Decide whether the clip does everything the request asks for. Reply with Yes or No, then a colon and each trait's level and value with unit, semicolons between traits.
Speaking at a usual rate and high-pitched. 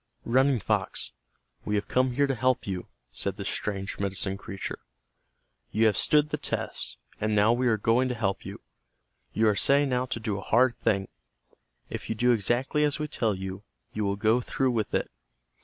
No: average, 190 wpm; low, 115 Hz